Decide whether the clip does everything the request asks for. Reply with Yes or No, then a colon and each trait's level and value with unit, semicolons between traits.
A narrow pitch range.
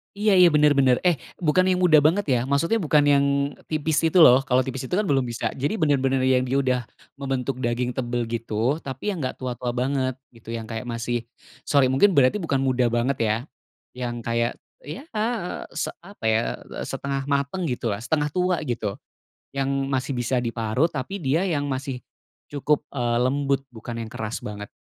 No: average, 3.6 semitones